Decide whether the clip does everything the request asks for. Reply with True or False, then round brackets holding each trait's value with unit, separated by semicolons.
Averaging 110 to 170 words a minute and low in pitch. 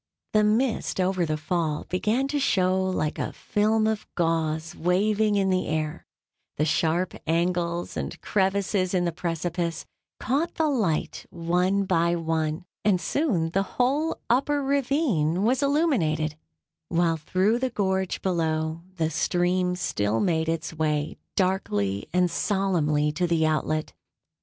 False (140 wpm; 180 Hz)